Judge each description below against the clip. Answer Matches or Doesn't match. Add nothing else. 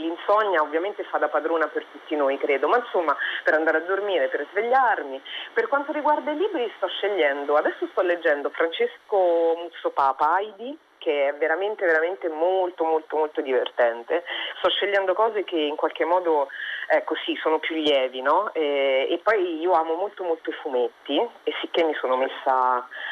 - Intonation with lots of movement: Matches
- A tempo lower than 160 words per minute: Doesn't match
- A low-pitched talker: Doesn't match